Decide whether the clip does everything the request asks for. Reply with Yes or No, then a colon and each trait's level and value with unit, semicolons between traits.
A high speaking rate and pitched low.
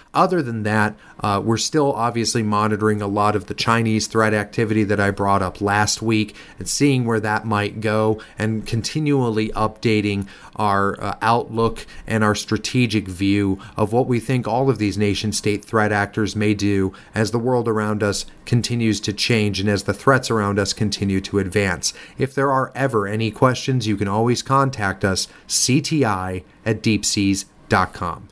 No: average, 170 wpm; low, 110 Hz